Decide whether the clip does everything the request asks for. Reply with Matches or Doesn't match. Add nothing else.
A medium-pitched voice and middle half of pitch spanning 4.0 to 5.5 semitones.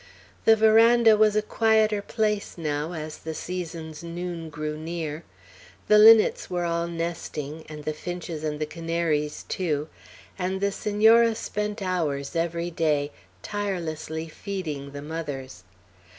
Matches